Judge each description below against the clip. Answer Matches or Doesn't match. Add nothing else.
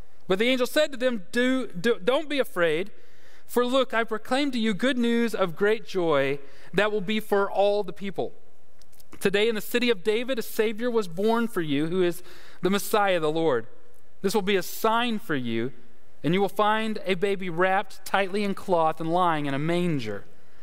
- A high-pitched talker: Matches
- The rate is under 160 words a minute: Doesn't match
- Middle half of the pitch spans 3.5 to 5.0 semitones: Matches